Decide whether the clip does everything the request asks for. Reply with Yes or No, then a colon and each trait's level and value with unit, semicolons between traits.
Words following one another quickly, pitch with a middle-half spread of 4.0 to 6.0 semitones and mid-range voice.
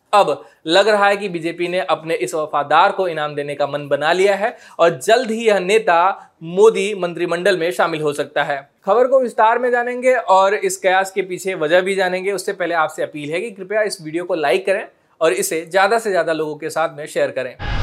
Yes: fast, 220 wpm; average, 4.3 semitones; medium, 180 Hz